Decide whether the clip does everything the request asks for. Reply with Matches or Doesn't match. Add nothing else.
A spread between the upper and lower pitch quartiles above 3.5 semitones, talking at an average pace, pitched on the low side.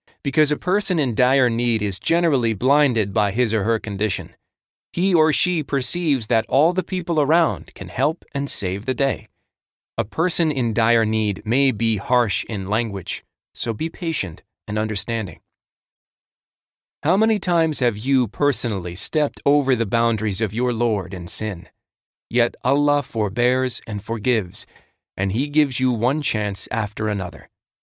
Matches